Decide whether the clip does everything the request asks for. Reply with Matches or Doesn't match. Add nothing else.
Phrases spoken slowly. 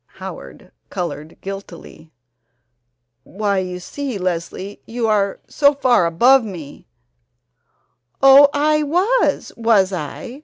Matches